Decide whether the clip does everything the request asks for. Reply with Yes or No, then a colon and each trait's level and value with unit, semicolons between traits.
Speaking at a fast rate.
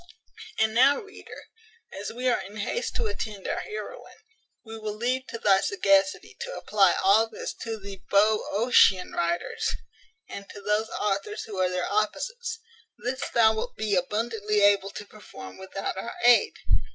No: average, 160 wpm